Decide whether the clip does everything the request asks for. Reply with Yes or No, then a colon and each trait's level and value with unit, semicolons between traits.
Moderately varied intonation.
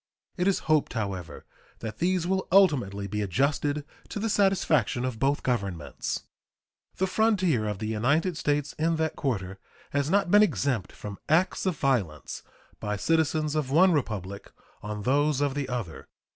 No: wide, 7.5 semitones